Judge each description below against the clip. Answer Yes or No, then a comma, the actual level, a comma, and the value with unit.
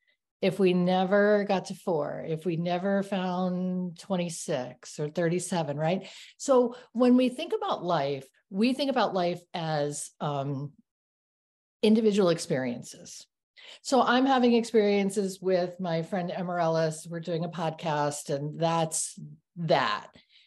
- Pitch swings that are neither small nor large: Yes, average, 4.1 semitones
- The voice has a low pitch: No, medium, 180 Hz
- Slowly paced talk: Yes, slow, 125 wpm